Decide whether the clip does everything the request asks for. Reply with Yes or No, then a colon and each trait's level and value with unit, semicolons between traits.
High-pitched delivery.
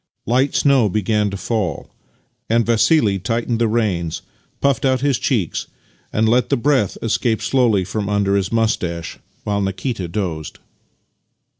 No: low, 110 Hz